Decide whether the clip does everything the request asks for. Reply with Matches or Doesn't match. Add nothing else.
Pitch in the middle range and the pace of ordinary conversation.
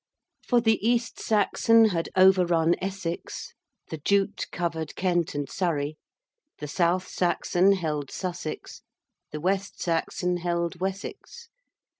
Doesn't match